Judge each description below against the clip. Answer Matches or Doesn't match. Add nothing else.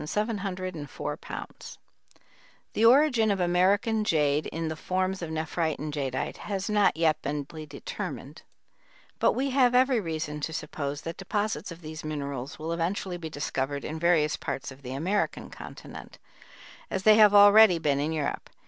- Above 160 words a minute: Doesn't match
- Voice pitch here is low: Doesn't match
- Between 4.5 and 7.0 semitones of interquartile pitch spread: Matches